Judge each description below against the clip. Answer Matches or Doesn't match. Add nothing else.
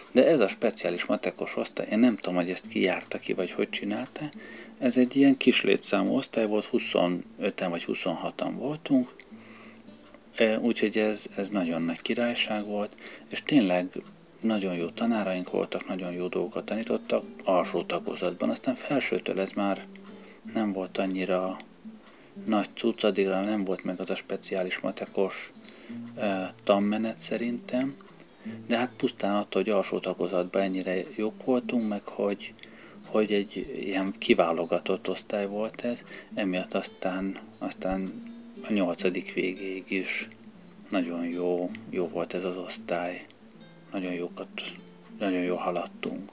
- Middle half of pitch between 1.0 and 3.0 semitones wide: Doesn't match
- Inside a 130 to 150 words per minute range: Matches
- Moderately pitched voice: Doesn't match